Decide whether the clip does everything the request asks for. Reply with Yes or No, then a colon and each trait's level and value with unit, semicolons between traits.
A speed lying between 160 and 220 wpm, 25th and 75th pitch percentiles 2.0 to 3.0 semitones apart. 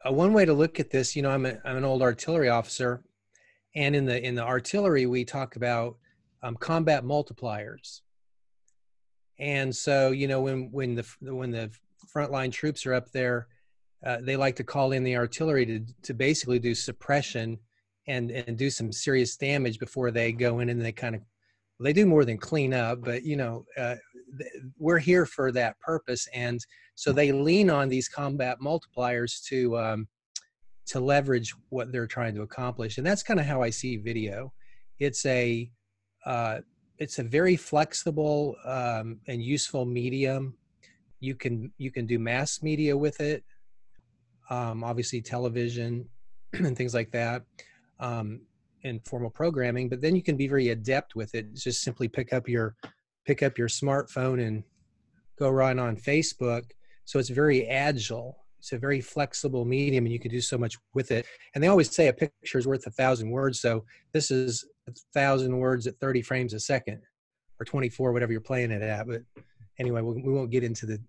Yes: average, 185 wpm; average, 2.7 semitones